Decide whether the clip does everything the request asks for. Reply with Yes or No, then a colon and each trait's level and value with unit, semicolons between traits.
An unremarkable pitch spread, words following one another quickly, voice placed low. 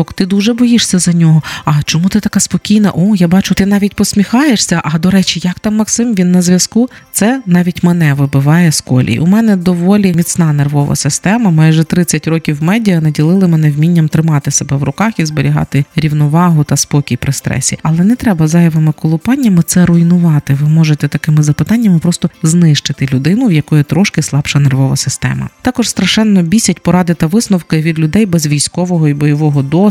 No: average, 4.3 semitones; fast, 175 wpm; medium, 170 Hz